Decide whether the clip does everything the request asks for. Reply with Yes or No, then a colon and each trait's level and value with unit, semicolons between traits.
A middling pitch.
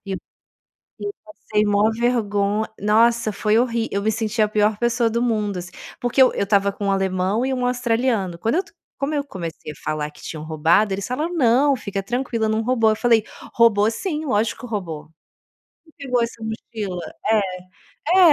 No: high, 220 Hz